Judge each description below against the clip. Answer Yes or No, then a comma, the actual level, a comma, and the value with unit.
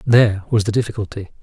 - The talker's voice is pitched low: Yes, low, 105 Hz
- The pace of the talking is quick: No, average, 170 wpm